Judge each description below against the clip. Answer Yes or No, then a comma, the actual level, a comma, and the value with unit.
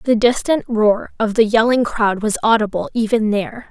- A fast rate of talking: No, average, 180 wpm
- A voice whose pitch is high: Yes, high, 220 Hz